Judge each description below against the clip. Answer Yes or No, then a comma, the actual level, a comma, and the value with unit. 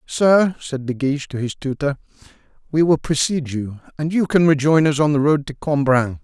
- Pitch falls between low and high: Yes, medium, 145 Hz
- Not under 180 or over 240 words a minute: Yes, average, 200 wpm